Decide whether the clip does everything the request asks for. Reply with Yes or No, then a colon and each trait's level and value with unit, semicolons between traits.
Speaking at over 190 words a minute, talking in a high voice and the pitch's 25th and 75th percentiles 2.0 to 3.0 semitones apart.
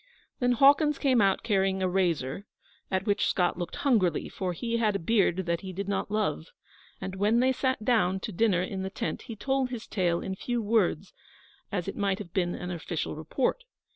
No: average, 200 wpm; high, 195 Hz; average, 4.3 semitones